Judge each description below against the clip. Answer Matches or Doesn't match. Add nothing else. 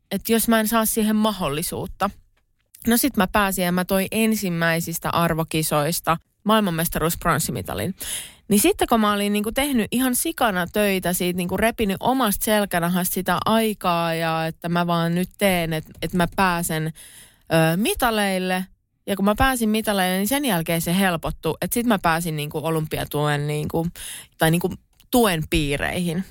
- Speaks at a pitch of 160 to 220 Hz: Matches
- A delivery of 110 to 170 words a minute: Matches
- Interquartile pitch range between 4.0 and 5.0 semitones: Matches